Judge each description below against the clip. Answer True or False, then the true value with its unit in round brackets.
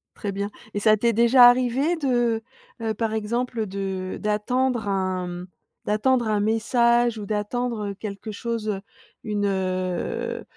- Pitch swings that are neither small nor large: True (3.0 semitones)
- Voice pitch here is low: False (215 Hz)